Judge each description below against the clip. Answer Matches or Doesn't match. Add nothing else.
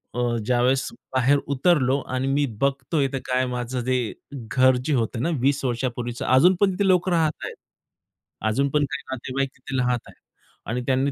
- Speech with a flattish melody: Matches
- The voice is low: Matches